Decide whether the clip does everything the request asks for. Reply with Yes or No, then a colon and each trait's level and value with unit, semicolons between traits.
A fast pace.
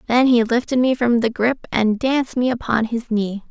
Yes: fast, 225 wpm